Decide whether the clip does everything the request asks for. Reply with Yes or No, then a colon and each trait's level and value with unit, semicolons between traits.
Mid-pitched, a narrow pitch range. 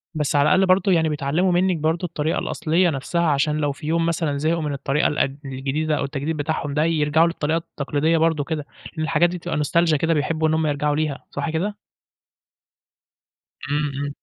Yes: medium, 155 Hz; narrow, 2.2 semitones